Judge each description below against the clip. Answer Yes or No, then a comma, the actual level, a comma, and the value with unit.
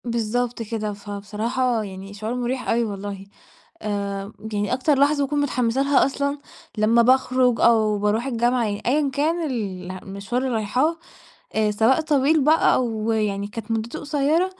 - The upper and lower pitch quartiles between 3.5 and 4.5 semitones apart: Yes, average, 4.1 semitones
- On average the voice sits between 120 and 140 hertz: No, high, 235 Hz